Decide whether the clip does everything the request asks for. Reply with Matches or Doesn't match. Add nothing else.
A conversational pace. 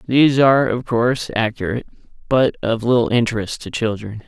Matches